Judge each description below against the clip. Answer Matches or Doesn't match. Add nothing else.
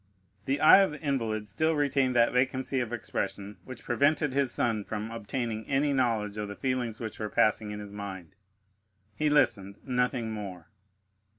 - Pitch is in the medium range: Doesn't match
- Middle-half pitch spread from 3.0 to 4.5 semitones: Matches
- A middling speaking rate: Matches